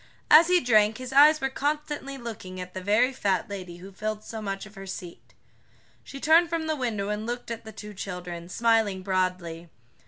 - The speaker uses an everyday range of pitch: No, wide, 6.0 semitones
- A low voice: No, high, 215 Hz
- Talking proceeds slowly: No, average, 195 wpm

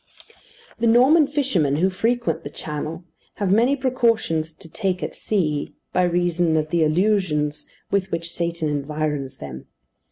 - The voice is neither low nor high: Yes, medium, 170 Hz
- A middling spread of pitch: No, wide, 5.7 semitones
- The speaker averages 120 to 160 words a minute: Yes, average, 140 wpm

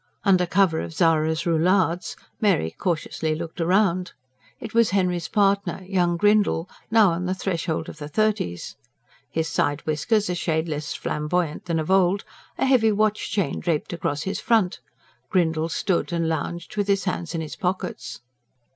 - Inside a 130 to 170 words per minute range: Yes, average, 160 wpm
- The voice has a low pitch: No, medium, 175 Hz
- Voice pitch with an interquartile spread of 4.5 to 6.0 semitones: No, average, 3.5 semitones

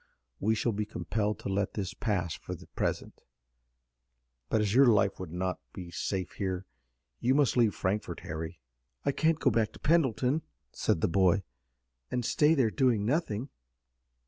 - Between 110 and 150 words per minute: No, average, 165 wpm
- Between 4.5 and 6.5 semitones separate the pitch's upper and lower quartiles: Yes, average, 5.0 semitones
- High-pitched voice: No, low, 105 Hz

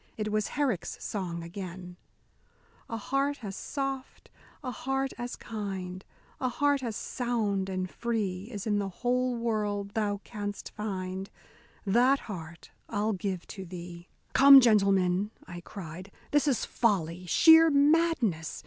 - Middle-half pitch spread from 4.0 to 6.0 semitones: Yes, average, 5.0 semitones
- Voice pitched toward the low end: No, high, 210 Hz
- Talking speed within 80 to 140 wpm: Yes, slow, 135 wpm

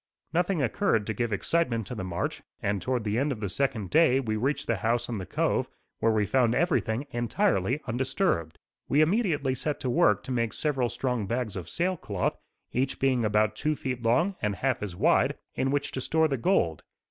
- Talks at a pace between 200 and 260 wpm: Yes, fast, 205 wpm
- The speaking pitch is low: Yes, low, 125 Hz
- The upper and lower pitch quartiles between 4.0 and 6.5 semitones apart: Yes, average, 4.6 semitones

